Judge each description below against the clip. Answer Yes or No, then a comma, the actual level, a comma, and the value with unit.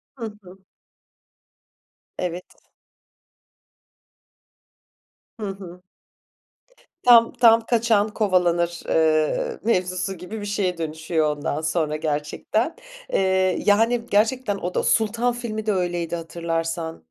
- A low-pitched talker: No, medium, 185 Hz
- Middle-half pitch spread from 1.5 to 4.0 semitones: No, average, 4.7 semitones